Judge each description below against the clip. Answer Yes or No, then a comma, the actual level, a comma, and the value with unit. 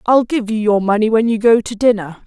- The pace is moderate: No, fast, 265 wpm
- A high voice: Yes, high, 220 Hz